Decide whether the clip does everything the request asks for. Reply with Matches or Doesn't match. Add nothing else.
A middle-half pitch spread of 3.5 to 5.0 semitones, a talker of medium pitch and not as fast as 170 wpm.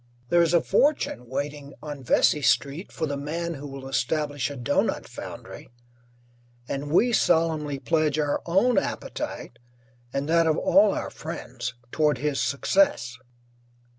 Doesn't match